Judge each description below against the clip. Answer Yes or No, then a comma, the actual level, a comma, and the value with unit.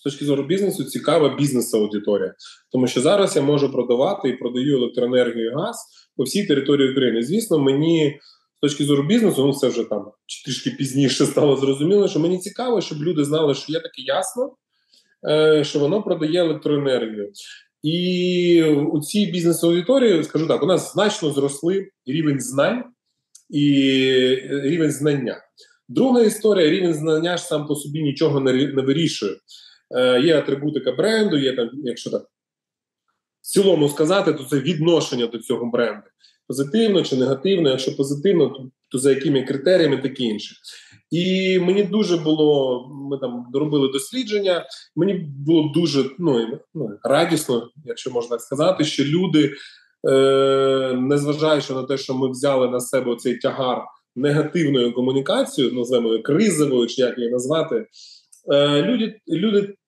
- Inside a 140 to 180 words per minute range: Yes, average, 145 wpm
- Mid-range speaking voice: Yes, medium, 145 Hz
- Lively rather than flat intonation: No, average, 4.8 semitones